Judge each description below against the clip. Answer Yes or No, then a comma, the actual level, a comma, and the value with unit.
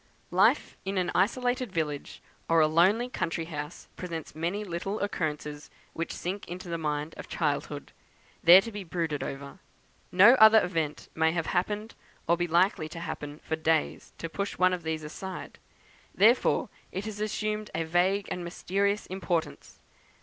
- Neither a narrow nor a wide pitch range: Yes, average, 3.8 semitones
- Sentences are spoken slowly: No, average, 160 wpm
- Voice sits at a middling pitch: Yes, medium, 175 Hz